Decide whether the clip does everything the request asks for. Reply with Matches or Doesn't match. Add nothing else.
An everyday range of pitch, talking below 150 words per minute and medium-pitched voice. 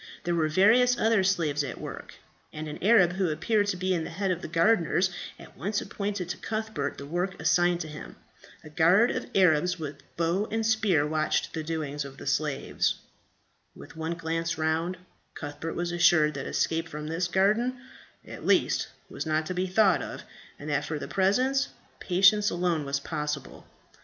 Doesn't match